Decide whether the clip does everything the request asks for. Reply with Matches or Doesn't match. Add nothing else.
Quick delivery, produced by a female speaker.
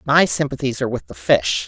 Matches